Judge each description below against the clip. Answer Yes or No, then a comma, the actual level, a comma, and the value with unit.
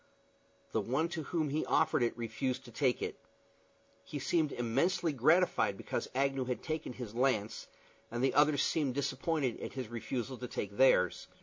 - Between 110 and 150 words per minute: No, average, 170 wpm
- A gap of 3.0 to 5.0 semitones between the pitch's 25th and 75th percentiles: Yes, average, 4.0 semitones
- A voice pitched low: Yes, low, 130 Hz